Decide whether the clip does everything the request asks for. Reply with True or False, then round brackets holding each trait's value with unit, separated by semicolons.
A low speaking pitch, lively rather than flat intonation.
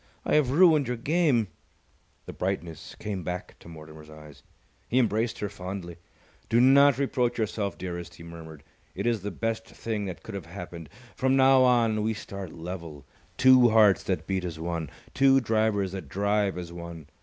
True (100 Hz; 5.7 semitones)